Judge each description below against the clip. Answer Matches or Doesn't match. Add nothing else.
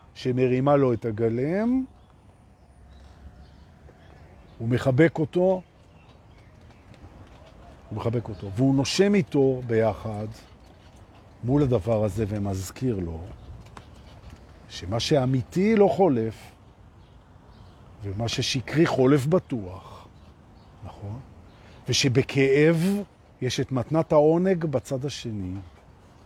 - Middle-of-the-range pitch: Doesn't match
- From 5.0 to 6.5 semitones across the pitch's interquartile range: Matches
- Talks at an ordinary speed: Doesn't match